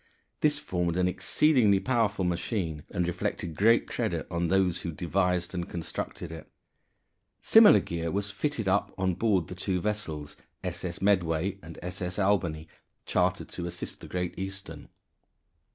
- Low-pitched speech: Yes, very low, 90 Hz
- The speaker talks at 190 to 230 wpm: No, average, 145 wpm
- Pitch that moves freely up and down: No, average, 2.8 semitones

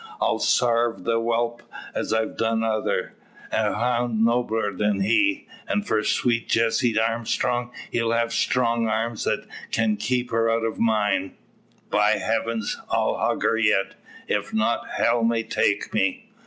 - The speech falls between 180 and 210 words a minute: No, average, 150 wpm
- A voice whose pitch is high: No, low, 115 Hz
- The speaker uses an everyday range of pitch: No, narrow, 1.3 semitones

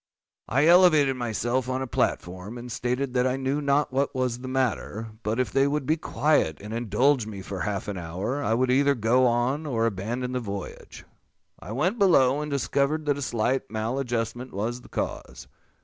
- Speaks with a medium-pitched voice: No, low, 125 Hz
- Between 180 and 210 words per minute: Yes, average, 190 wpm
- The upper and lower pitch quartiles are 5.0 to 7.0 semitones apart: No, average, 3.5 semitones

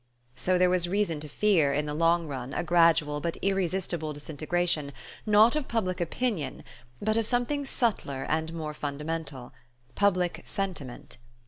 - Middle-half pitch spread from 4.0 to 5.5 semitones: Yes, average, 4.7 semitones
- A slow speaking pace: No, average, 145 wpm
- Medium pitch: Yes, medium, 170 Hz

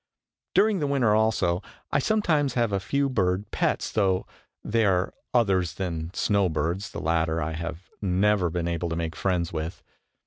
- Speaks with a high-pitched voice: No, very low, 95 Hz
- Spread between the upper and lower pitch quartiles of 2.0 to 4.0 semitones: No, average, 4.6 semitones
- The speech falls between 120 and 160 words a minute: No, average, 170 wpm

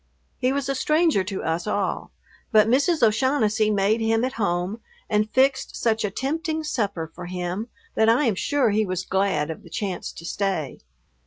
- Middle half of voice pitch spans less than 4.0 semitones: No, wide, 5.4 semitones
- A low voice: No, high, 215 Hz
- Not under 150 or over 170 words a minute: No, average, 180 wpm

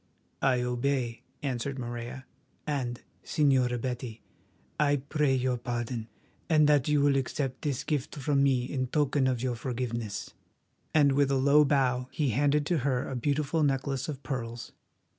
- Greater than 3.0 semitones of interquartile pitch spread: No, narrow, 2.6 semitones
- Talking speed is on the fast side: No, average, 155 wpm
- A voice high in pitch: No, low, 135 Hz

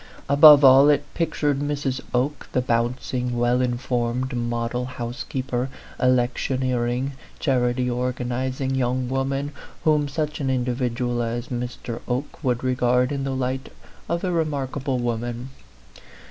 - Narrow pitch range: Yes, narrow, 1.9 semitones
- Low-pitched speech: Yes, low, 130 Hz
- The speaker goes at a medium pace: No, slow, 125 wpm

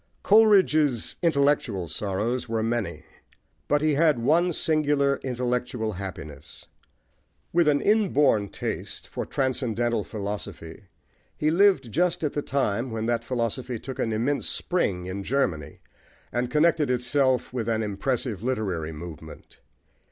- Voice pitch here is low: Yes, low, 125 Hz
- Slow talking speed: Yes, slow, 125 wpm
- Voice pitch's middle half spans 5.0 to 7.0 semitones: Yes, average, 5.3 semitones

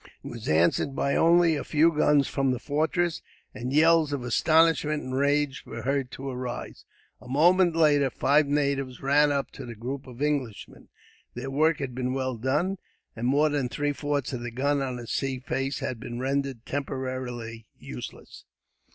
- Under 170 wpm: No, average, 175 wpm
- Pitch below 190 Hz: Yes, low, 135 Hz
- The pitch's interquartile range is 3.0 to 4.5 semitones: No, narrow, 2.6 semitones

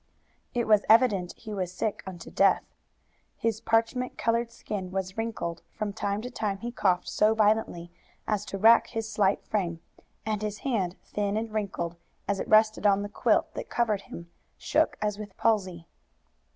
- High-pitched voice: Yes, high, 210 Hz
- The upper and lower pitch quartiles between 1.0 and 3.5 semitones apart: Yes, narrow, 2.5 semitones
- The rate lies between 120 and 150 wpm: No, average, 170 wpm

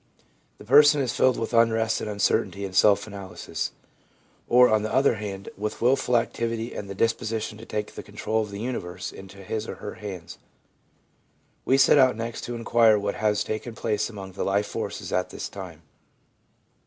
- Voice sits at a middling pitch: No, low, 110 Hz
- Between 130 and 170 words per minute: No, average, 180 wpm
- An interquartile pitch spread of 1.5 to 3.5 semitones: Yes, average, 2.7 semitones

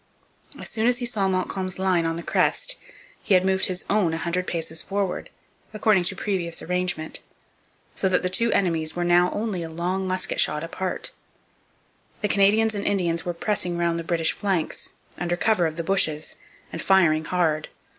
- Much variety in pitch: No, average, 2.7 semitones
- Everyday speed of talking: Yes, average, 180 wpm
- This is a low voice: No, medium, 180 Hz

